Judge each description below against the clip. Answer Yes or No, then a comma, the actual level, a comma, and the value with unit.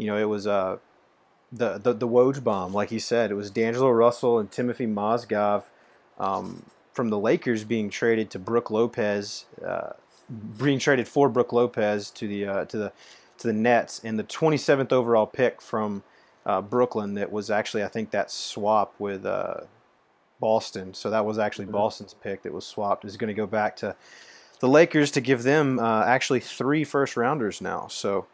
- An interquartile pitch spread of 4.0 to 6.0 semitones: No, average, 3.0 semitones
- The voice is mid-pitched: No, low, 115 Hz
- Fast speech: No, average, 185 wpm